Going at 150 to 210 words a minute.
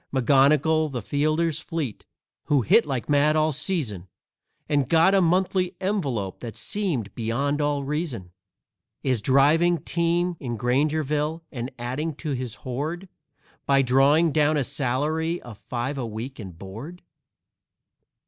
No: slow, 135 wpm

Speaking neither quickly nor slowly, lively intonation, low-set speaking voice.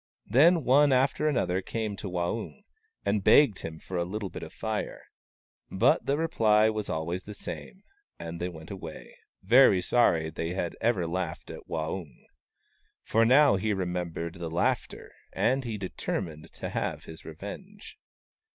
Yes: average, 160 wpm; wide, 6.0 semitones; very low, 95 Hz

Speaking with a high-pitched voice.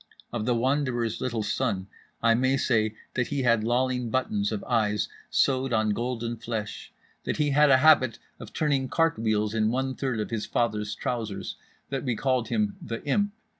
No: low, 120 Hz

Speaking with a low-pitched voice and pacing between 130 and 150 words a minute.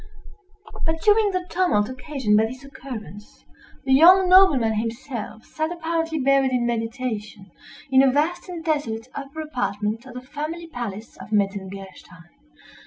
No: very high, 260 Hz; average, 140 wpm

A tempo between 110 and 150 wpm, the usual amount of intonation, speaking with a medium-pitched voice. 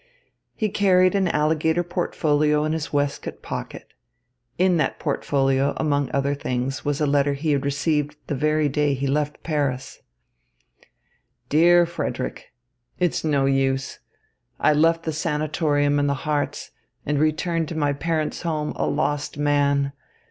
No: average, 140 wpm; narrow, 2.1 semitones; medium, 150 Hz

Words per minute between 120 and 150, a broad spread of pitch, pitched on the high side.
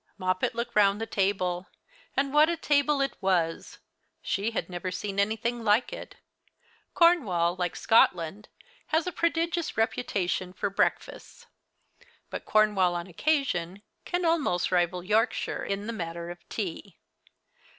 Yes: slow, 135 wpm; wide, 7.1 semitones; high, 205 Hz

